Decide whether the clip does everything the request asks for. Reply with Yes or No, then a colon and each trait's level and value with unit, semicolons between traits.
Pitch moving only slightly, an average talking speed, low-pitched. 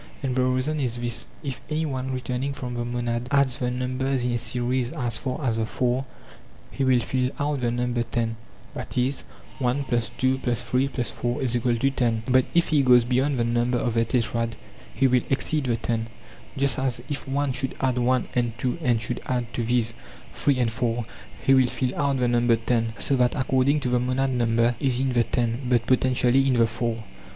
Yes: narrow, 1.8 semitones; average, 190 wpm; low, 125 Hz